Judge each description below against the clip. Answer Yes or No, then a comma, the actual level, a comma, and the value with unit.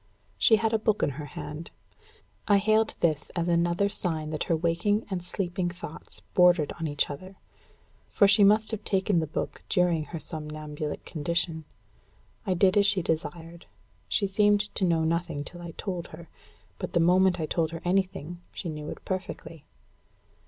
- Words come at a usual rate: Yes, average, 175 wpm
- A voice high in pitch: No, medium, 175 Hz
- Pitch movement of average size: Yes, average, 3.4 semitones